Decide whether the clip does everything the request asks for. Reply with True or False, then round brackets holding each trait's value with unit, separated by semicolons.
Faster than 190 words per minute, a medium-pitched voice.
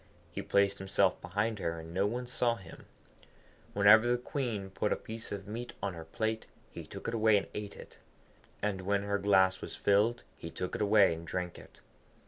False (200 wpm; 100 Hz)